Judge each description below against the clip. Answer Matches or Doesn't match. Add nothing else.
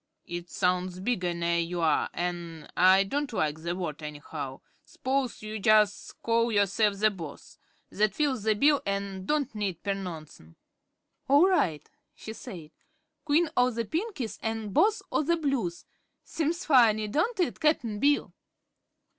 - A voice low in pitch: Doesn't match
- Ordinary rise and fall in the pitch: Doesn't match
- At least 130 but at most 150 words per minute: Matches